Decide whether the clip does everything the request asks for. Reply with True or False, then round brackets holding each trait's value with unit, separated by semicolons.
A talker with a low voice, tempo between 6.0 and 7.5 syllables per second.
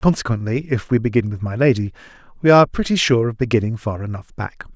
True (120 Hz; 6.2 syllables/s)